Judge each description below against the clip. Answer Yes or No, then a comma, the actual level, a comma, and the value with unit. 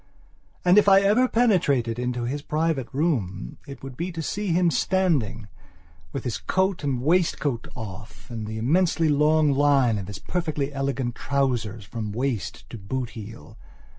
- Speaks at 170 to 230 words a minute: No, average, 160 wpm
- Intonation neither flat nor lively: No, wide, 6.1 semitones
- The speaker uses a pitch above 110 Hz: Yes, low, 135 Hz